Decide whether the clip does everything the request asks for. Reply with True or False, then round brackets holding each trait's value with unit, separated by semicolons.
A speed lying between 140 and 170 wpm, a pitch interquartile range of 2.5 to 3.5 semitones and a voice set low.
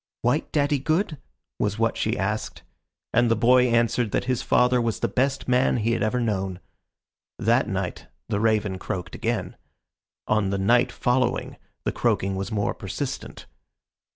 True (155 wpm; 3.2 semitones; 115 Hz)